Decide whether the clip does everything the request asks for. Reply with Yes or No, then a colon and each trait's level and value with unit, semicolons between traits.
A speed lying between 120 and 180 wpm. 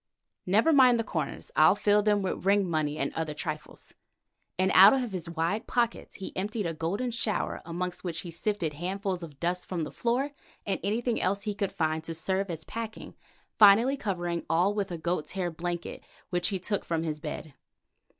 No: average, 190 wpm